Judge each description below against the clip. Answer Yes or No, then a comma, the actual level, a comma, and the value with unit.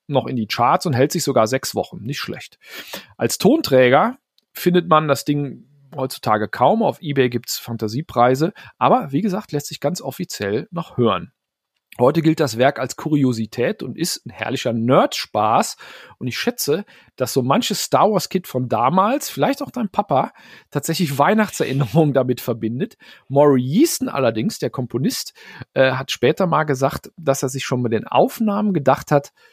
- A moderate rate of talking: Yes, average, 165 wpm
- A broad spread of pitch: Yes, wide, 5.7 semitones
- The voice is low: No, medium, 145 Hz